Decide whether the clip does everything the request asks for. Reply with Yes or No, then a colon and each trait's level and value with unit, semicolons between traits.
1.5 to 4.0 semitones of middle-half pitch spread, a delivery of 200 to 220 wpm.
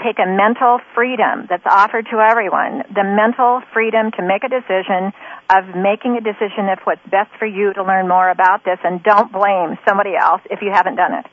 Yes: average, 2.9 semitones; fast, 205 wpm